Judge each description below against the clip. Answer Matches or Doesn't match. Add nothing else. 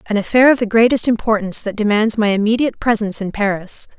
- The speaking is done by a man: Doesn't match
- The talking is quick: Doesn't match